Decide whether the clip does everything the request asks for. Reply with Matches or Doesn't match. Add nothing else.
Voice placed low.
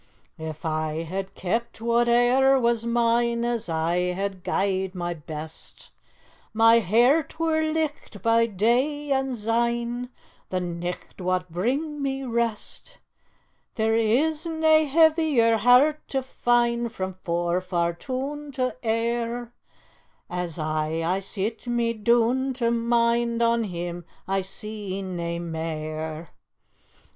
Doesn't match